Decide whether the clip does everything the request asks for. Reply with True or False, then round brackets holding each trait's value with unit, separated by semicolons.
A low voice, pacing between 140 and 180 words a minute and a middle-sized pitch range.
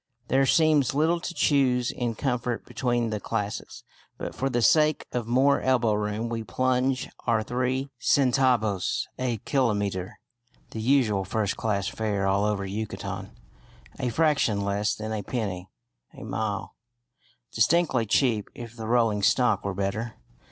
True (115 Hz; 145 wpm; 3.7 semitones)